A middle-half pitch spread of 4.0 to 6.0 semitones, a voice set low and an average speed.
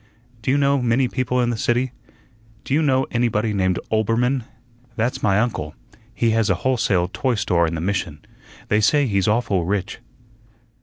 Yes: average, 4.3 semitones; low, 115 Hz; average, 170 wpm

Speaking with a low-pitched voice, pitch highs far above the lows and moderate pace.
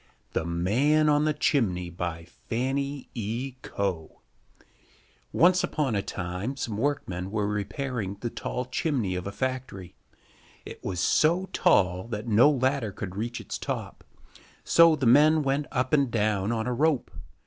Yes: low, 120 Hz; wide, 5.9 semitones; average, 150 wpm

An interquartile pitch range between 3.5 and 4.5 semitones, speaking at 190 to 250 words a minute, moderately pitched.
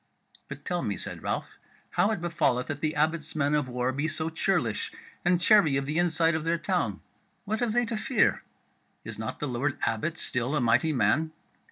Yes: average, 3.8 semitones; average, 200 wpm; medium, 155 Hz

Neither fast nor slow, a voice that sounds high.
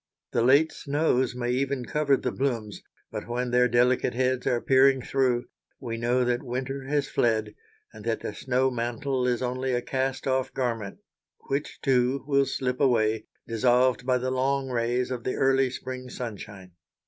No: average, 170 wpm; low, 125 Hz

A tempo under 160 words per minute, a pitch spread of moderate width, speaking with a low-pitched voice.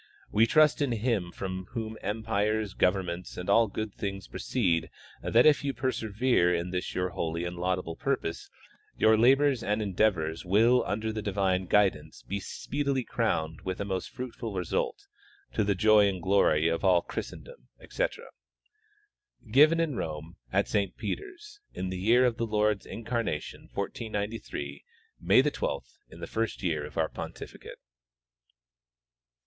Yes: average, 150 wpm; average, 4.2 semitones; low, 105 Hz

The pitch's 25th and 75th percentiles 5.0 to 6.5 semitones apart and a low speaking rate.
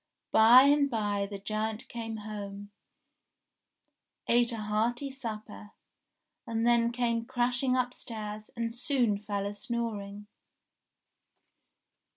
No: narrow, 2.5 semitones; slow, 105 wpm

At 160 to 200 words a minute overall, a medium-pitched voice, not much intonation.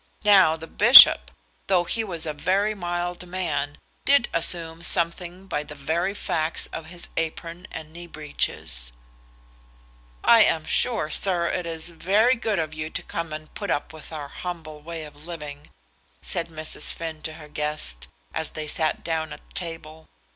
Yes: average, 165 wpm; medium, 165 Hz; narrow, 2.3 semitones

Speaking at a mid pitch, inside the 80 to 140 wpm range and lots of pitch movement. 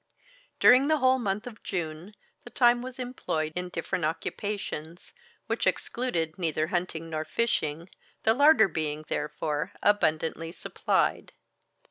Yes: medium, 180 Hz; slow, 135 wpm; wide, 7.2 semitones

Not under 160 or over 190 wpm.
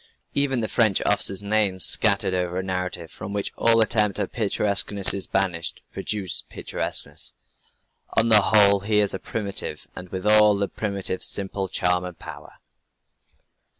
No: average, 150 wpm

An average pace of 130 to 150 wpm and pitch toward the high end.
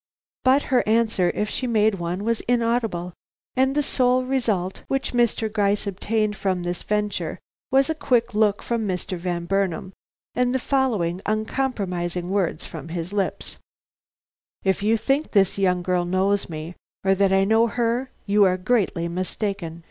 No: average, 160 wpm; high, 205 Hz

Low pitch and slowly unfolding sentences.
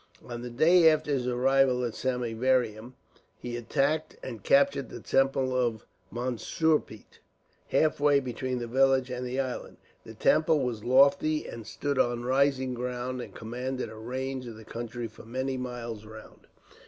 No: low, 125 Hz; average, 155 wpm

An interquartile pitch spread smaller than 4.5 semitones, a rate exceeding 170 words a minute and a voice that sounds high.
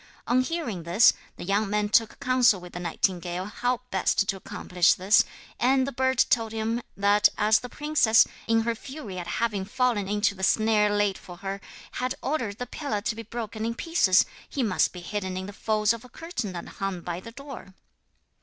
Yes: average, 4.0 semitones; average, 200 wpm; high, 215 Hz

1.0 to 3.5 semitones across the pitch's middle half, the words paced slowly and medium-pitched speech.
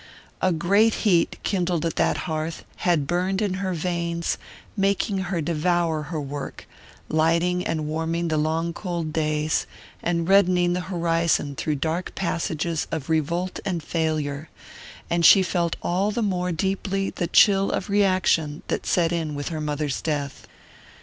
No: average, 2.7 semitones; average, 150 wpm; medium, 170 Hz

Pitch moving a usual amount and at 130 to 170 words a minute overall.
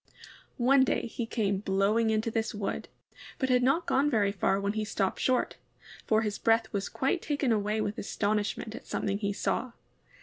No: average, 3.4 semitones; average, 180 wpm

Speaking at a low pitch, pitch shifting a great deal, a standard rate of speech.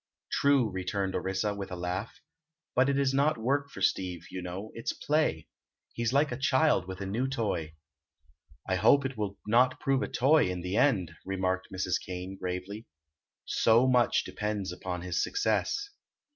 Yes: low, 105 Hz; wide, 6.1 semitones; average, 170 wpm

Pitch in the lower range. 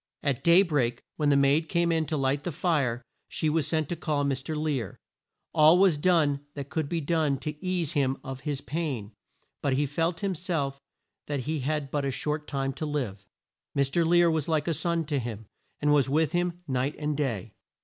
No: medium, 150 Hz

